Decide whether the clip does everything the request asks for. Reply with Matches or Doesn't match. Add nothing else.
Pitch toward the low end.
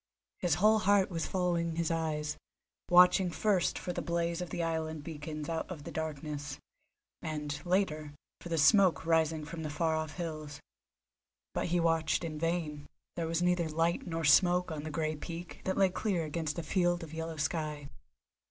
Doesn't match